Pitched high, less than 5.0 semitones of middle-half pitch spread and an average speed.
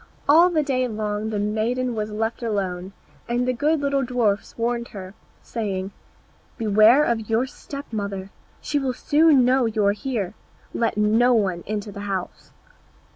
Yes: high, 225 Hz; average, 3.7 semitones; average, 160 wpm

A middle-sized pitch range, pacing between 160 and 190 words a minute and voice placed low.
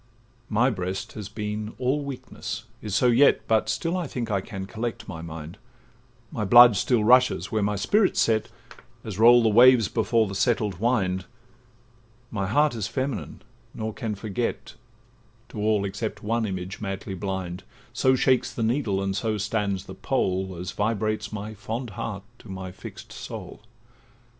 Yes: average, 3.4 semitones; average, 165 wpm; low, 110 Hz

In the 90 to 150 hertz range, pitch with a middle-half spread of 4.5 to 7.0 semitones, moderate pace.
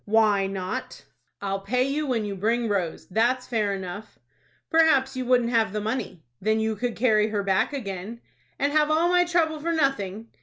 No: high, 225 Hz; average, 4.9 semitones; average, 185 wpm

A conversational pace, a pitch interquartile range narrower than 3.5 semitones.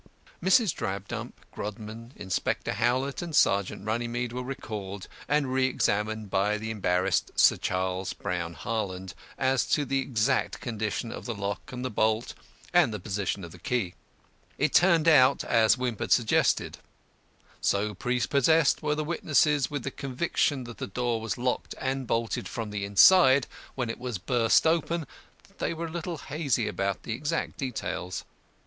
No: average, 160 wpm; average, 4.8 semitones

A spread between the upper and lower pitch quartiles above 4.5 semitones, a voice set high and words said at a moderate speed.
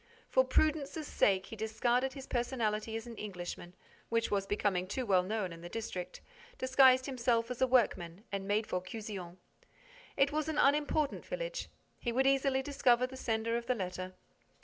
Yes: average, 4.9 semitones; high, 230 Hz; average, 170 wpm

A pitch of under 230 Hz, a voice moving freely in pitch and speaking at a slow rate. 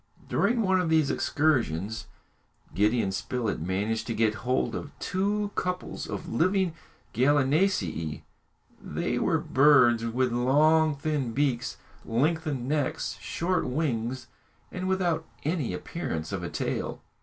Yes: medium, 140 Hz; wide, 5.9 semitones; slow, 120 wpm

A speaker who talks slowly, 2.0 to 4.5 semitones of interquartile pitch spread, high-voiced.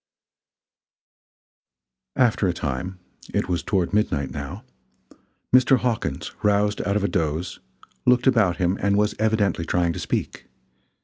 No: slow, 130 wpm; average, 3.8 semitones; low, 100 Hz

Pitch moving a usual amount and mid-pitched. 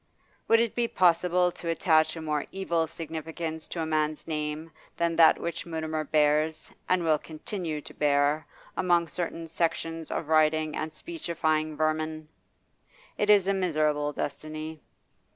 No: narrow, 1.6 semitones; medium, 160 Hz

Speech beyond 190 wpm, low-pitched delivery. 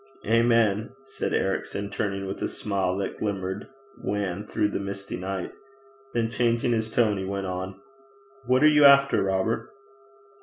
No: average, 150 wpm; low, 100 Hz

